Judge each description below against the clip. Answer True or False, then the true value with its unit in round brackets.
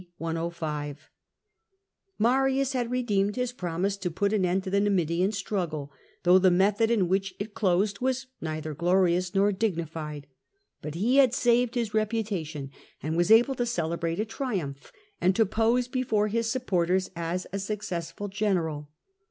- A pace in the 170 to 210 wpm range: False (150 wpm)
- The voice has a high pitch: True (195 Hz)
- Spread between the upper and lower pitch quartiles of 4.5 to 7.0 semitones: True (4.8 semitones)